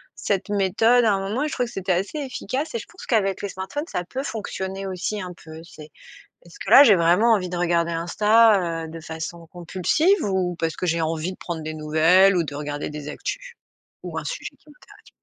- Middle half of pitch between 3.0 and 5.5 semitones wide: Yes, average, 5.0 semitones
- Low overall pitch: No, medium, 185 Hz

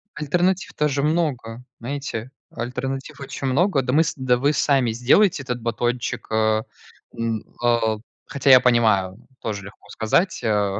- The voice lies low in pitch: Yes, low, 125 Hz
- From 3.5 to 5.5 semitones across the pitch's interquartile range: Yes, average, 3.9 semitones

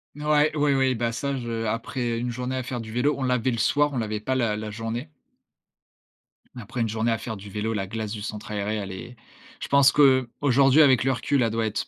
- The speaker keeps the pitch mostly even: No, average, 3.3 semitones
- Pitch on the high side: No, low, 120 Hz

